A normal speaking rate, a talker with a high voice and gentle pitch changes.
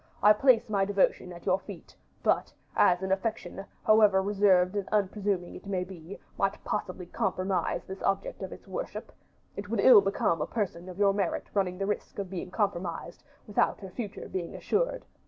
Yes: average, 180 wpm; high, 195 Hz; narrow, 2.1 semitones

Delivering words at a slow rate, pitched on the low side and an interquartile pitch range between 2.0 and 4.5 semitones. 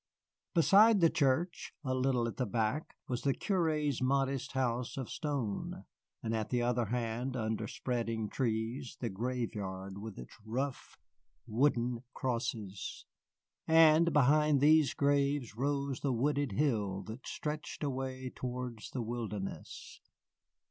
Yes: slow, 125 wpm; low, 125 Hz; average, 3.8 semitones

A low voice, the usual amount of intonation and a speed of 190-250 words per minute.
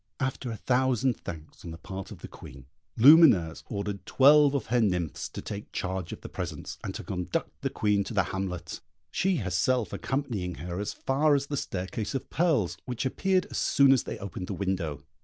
No: low, 105 Hz; wide, 6.8 semitones; average, 195 wpm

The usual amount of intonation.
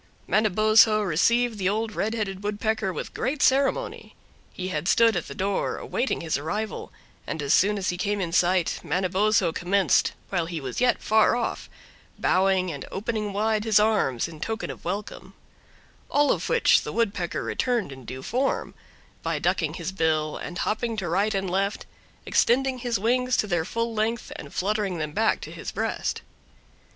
Yes: average, 3.8 semitones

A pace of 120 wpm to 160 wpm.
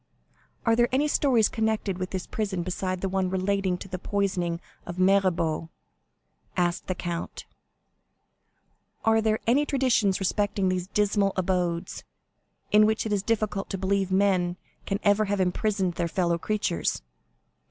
Yes: average, 140 wpm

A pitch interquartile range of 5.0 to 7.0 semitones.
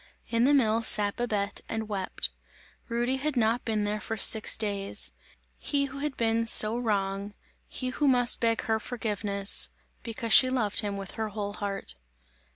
No: average, 2.9 semitones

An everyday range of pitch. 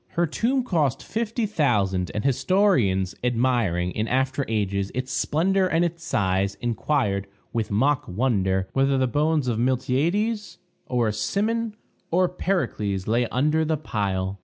No: wide, 8.4 semitones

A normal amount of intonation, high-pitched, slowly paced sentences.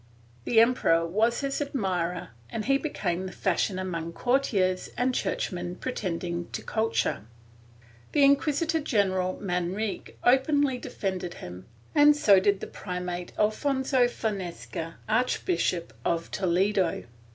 No: wide, 6.1 semitones; high, 200 Hz; slow, 120 wpm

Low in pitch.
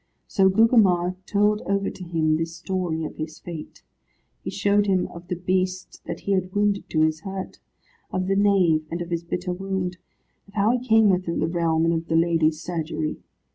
No: medium, 180 Hz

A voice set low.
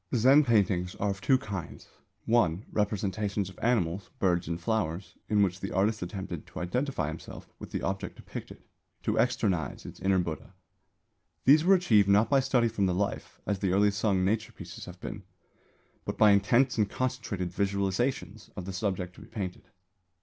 Yes: low, 100 Hz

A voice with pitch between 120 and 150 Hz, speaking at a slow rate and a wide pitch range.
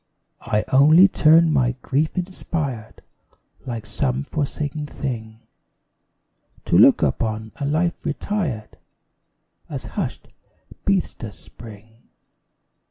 Yes: medium, 140 Hz; slow, 95 wpm; wide, 5.7 semitones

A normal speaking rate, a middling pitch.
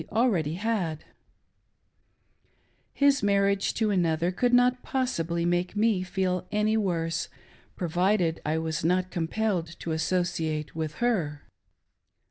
No: slow, 115 wpm; medium, 180 Hz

